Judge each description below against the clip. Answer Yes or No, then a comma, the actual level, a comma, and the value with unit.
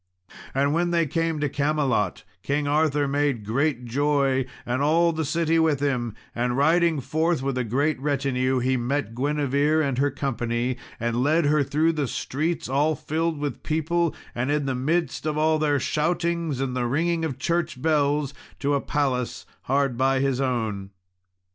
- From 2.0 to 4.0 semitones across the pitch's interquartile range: Yes, average, 3.2 semitones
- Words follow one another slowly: No, average, 170 wpm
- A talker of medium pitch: Yes, medium, 145 Hz